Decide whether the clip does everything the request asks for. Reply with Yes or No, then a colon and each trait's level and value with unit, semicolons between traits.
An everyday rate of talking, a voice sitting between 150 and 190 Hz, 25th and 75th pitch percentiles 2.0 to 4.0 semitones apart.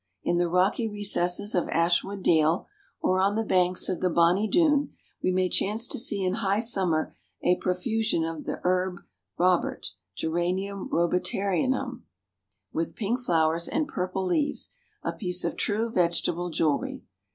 Yes: average, 150 wpm; medium, 185 Hz; average, 3.1 semitones